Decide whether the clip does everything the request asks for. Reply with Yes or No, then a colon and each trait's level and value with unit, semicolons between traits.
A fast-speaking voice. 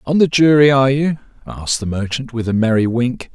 Yes: fast, 215 wpm